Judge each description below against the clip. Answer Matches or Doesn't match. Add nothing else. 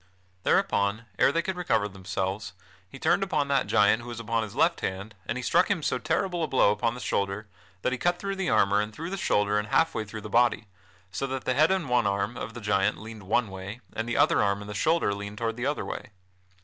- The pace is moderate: Doesn't match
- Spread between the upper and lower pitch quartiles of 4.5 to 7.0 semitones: Matches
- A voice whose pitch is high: Doesn't match